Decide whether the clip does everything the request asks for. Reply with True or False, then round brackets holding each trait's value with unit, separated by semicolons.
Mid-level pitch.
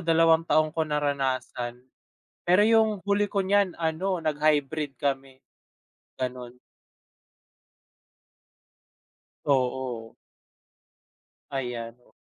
True (150 Hz)